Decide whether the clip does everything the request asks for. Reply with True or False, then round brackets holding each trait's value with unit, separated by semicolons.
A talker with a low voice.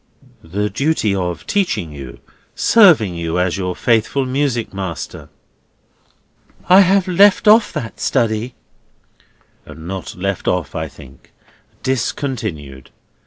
True (105 Hz)